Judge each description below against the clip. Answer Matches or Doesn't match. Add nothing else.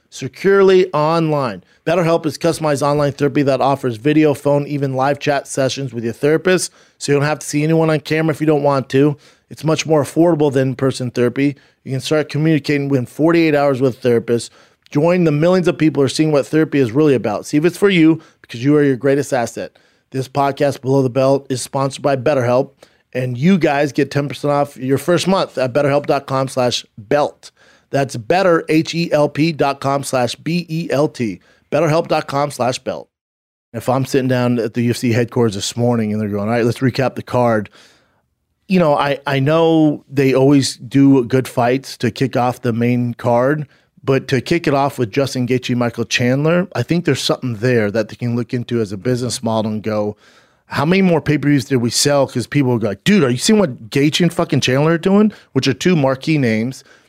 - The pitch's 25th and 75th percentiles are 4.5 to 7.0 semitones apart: Doesn't match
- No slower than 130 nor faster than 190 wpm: Doesn't match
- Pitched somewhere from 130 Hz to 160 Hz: Matches